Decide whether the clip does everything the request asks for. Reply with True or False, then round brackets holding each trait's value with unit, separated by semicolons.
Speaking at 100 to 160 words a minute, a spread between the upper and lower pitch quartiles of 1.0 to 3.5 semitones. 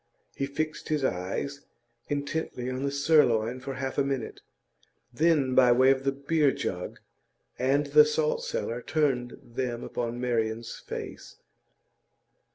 True (135 wpm; 2.8 semitones)